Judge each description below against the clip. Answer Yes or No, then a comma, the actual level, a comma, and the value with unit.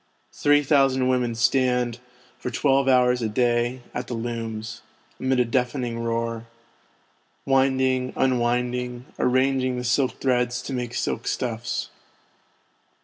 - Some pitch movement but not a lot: No, narrow, 1.5 semitones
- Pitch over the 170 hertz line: No, low, 125 Hz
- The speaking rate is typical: No, slow, 120 wpm